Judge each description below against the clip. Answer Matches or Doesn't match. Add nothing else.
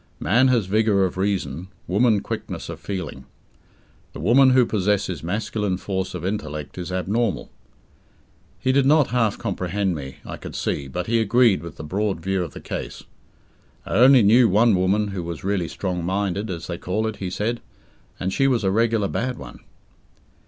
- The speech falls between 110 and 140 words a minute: Doesn't match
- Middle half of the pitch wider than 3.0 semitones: Matches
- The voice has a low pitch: Matches